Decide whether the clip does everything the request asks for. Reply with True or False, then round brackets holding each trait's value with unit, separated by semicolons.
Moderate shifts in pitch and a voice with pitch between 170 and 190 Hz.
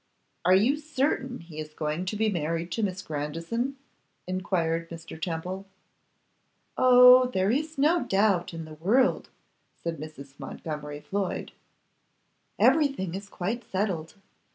False (6.5 semitones; 185 Hz)